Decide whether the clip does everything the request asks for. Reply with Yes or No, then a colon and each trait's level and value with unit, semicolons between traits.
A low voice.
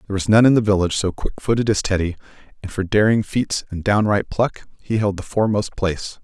Yes: low, 100 Hz